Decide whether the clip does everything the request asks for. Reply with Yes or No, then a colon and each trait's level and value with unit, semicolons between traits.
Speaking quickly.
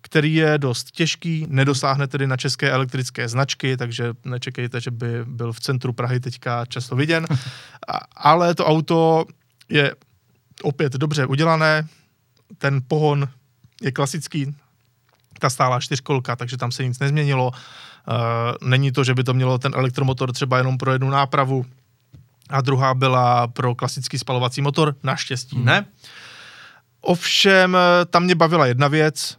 No: average, 140 wpm